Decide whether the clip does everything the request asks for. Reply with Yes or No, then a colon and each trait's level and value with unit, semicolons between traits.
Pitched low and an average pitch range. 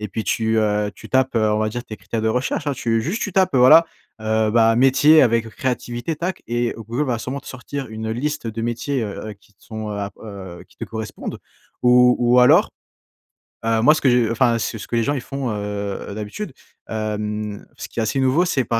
Yes: low, 115 Hz; average, 3.3 semitones